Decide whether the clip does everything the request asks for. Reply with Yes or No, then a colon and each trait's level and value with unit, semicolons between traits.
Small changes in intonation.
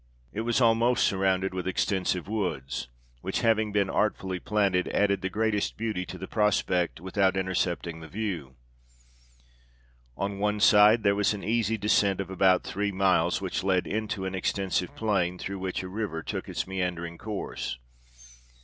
Yes: narrow, 2.3 semitones